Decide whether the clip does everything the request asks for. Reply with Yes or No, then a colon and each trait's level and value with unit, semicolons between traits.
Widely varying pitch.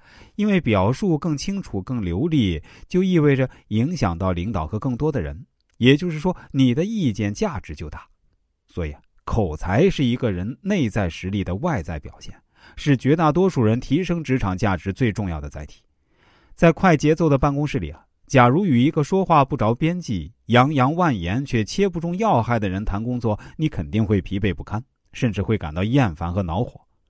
Yes: wide, 7.6 semitones